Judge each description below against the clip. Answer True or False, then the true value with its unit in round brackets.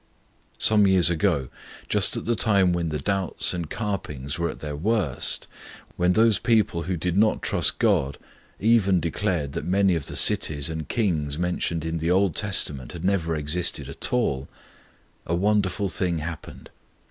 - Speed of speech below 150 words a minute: False (165 wpm)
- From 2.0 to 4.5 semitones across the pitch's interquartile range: True (4.2 semitones)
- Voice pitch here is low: True (90 Hz)